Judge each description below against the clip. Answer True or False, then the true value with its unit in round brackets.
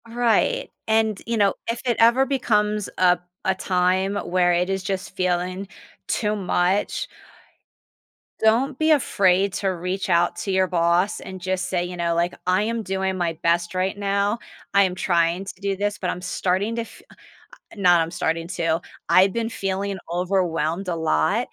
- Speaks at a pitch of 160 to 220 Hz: True (190 Hz)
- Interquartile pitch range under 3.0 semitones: True (2.6 semitones)